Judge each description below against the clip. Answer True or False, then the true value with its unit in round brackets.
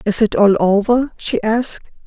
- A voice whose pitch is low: False (215 Hz)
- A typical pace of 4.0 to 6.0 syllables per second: True (4.5 syllables/s)